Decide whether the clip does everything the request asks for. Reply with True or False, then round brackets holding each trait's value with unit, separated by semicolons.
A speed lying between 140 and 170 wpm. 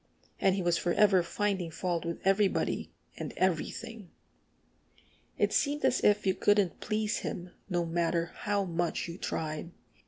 True (145 wpm)